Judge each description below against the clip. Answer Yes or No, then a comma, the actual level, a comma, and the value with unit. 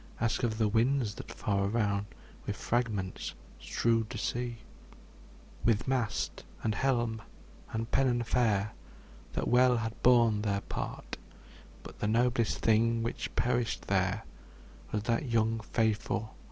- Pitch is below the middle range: Yes, low, 115 Hz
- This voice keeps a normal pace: No, slow, 130 wpm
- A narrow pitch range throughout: Yes, narrow, 2.2 semitones